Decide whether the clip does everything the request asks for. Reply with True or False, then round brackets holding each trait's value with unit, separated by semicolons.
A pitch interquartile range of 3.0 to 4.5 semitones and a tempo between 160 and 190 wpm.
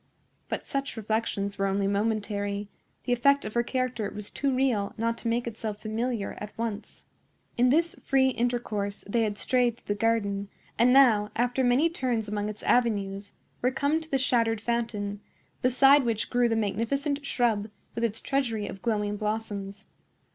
True (3.3 semitones; 170 wpm)